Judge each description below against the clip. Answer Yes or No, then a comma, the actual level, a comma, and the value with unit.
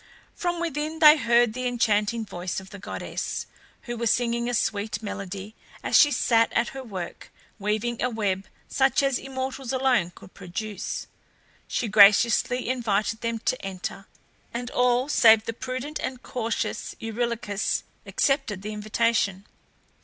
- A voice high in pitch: Yes, high, 230 Hz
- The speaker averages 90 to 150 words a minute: Yes, average, 145 wpm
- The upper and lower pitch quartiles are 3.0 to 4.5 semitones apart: Yes, average, 3.5 semitones